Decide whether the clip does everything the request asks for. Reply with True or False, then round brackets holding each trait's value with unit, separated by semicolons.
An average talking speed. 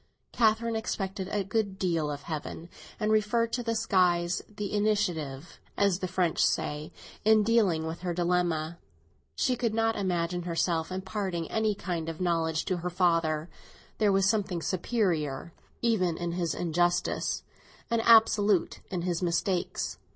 True (145 wpm)